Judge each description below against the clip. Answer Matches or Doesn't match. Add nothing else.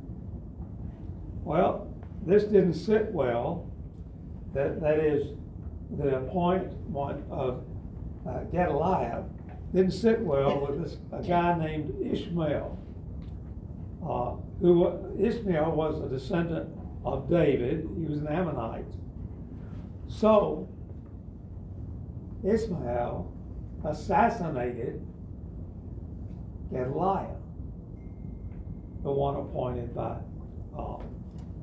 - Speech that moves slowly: Matches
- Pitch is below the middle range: Matches